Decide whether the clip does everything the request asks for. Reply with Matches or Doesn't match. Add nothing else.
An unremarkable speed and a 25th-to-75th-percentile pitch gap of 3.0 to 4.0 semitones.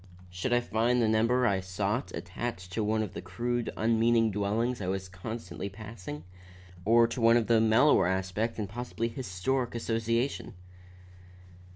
Matches